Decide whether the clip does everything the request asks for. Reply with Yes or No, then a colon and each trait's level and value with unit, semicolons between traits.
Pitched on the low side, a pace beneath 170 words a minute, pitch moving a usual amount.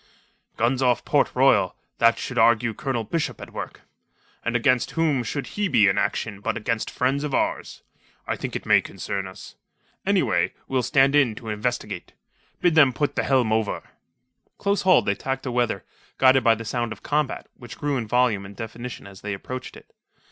No: low, 120 Hz; average, 185 wpm; average, 3.3 semitones